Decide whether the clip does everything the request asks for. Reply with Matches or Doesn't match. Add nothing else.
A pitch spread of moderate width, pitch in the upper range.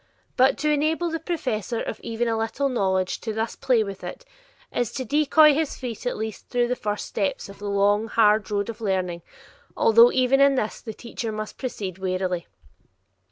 Matches